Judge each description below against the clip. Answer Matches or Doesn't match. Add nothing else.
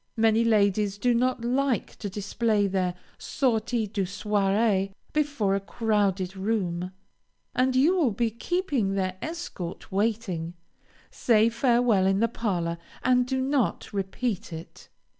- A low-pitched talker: Doesn't match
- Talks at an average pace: Doesn't match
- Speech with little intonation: Doesn't match